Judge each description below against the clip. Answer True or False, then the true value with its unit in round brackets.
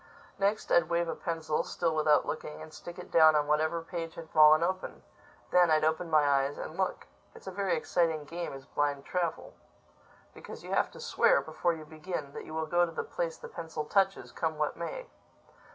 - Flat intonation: True (2.1 semitones)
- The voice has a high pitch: False (160 Hz)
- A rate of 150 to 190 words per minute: False (205 wpm)